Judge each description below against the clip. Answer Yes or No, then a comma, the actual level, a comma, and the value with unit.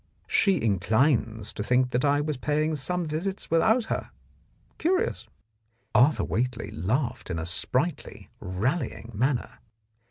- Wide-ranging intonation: Yes, wide, 5.8 semitones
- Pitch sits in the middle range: No, low, 130 Hz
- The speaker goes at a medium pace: No, slow, 130 wpm